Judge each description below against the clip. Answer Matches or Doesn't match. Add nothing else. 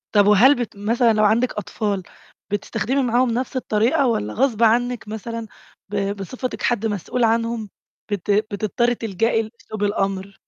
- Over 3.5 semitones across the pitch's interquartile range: Doesn't match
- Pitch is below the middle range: Doesn't match